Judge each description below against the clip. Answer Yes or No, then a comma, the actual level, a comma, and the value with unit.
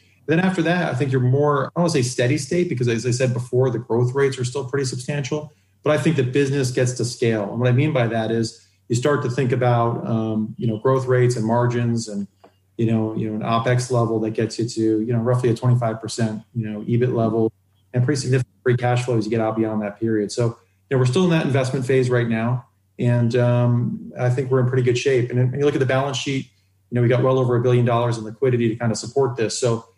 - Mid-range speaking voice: No, low, 120 Hz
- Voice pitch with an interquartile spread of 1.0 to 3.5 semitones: Yes, average, 2.8 semitones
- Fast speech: Yes, fast, 255 wpm